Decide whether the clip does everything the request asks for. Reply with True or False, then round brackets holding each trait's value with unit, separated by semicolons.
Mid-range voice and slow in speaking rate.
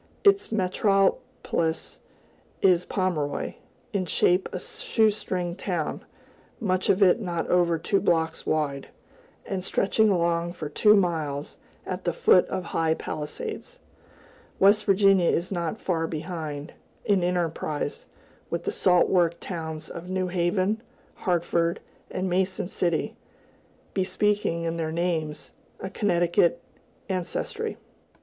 True (180 Hz; 120 wpm)